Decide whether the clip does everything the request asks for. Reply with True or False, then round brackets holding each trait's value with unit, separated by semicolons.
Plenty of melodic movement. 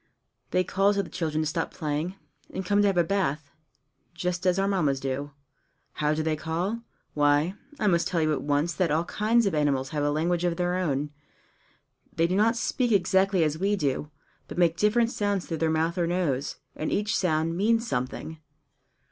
False (4.2 semitones)